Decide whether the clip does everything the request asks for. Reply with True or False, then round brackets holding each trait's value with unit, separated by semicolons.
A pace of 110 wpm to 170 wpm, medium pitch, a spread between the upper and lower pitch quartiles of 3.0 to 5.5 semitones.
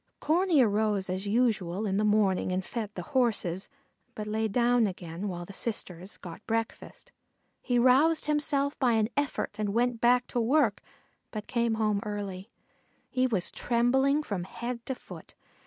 False (160 wpm; 225 Hz; 3.8 semitones)